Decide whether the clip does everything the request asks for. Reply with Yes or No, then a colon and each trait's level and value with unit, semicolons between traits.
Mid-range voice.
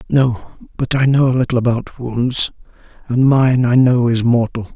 No: low, 125 Hz